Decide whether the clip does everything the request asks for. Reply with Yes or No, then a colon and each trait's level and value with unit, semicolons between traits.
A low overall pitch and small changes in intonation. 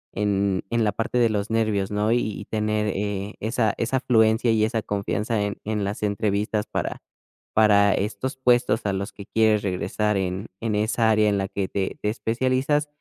Yes: low, 105 Hz; narrow, 1.8 semitones